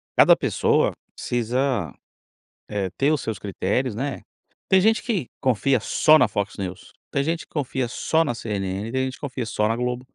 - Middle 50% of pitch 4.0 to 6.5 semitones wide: Yes, average, 4.7 semitones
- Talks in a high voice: No, low, 125 Hz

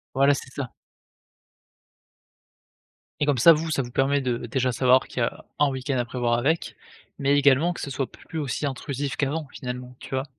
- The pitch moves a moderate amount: No, narrow, 2.2 semitones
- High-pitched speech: No, low, 135 Hz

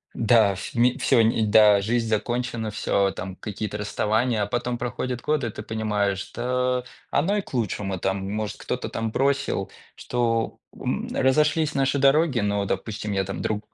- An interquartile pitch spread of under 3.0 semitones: No, average, 3.4 semitones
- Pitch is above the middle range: No, low, 110 Hz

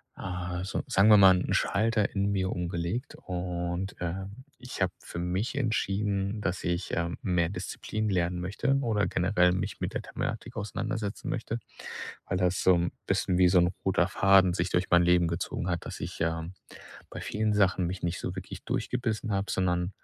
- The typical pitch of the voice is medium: No, very low, 95 Hz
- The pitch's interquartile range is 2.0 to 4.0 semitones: Yes, narrow, 2.6 semitones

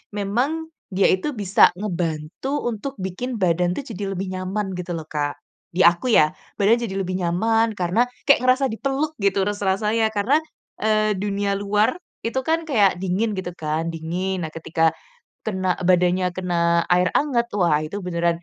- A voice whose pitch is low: No, high, 195 Hz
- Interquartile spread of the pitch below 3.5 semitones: No, average, 4.2 semitones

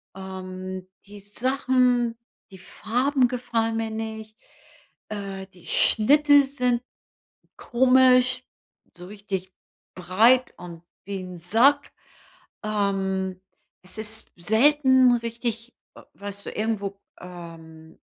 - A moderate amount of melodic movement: Yes, average, 4.7 semitones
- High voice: Yes, high, 220 Hz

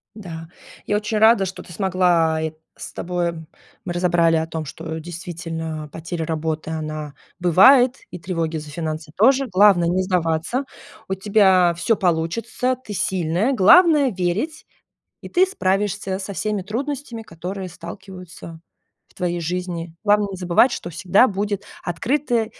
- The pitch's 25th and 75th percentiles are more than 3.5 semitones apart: Yes, average, 4.1 semitones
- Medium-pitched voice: Yes, medium, 180 Hz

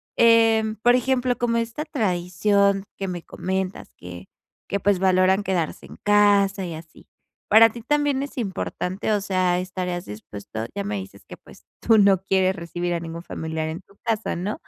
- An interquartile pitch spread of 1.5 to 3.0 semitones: No, average, 3.7 semitones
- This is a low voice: No, high, 195 Hz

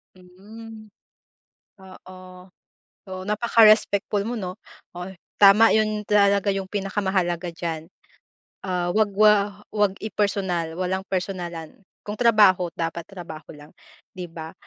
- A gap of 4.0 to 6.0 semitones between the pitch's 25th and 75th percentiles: No, narrow, 2.6 semitones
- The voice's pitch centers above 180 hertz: Yes, high, 190 Hz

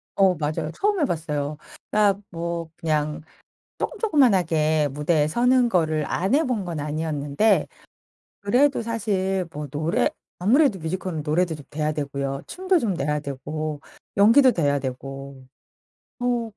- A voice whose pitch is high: No, medium, 165 Hz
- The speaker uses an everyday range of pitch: No, wide, 6.4 semitones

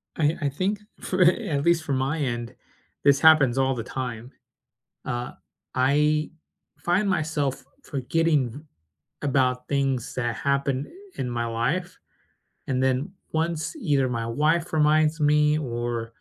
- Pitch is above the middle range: No, medium, 140 Hz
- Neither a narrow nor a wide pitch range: Yes, average, 3.8 semitones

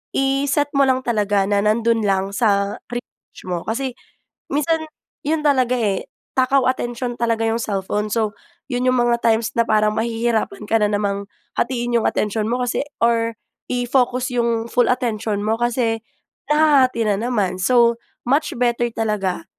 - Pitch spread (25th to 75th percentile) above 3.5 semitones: No, average, 2.9 semitones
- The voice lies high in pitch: Yes, high, 235 Hz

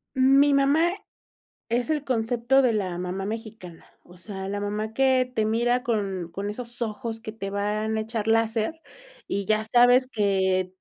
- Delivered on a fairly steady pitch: No, average, 3.4 semitones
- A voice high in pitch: Yes, high, 220 Hz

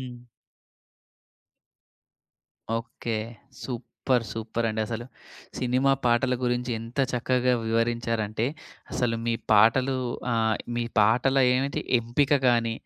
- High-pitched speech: No, low, 120 Hz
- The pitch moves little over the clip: Yes, narrow, 1.7 semitones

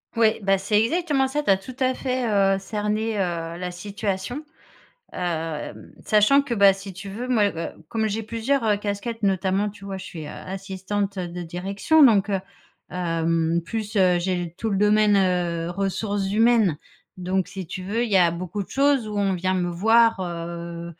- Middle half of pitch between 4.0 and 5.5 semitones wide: No, average, 3.5 semitones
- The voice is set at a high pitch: Yes, high, 195 Hz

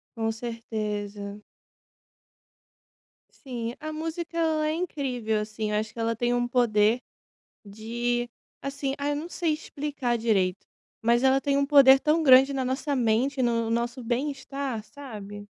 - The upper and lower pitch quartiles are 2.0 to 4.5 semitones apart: Yes, average, 4.0 semitones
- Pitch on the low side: No, high, 245 Hz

